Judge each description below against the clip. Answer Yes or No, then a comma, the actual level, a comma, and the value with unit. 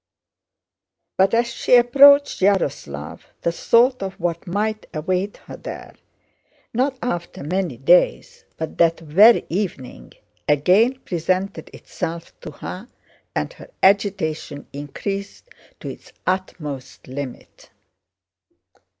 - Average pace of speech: No, slow, 100 wpm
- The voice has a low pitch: No, medium, 185 Hz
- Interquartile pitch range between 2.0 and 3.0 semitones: No, average, 5.2 semitones